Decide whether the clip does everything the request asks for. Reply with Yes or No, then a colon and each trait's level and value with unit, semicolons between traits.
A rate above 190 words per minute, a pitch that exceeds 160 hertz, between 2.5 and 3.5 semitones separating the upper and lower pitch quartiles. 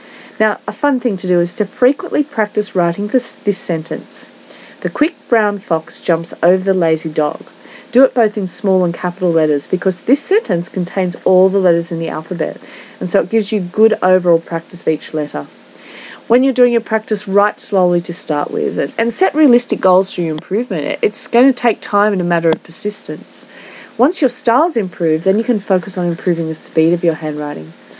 No: average, 200 wpm; high, 190 Hz; average, 5.2 semitones